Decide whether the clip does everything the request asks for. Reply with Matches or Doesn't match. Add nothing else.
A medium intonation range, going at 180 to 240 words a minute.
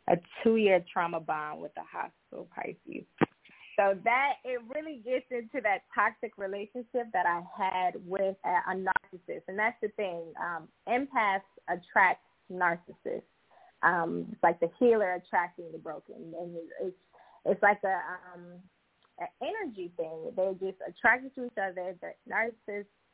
Doesn't match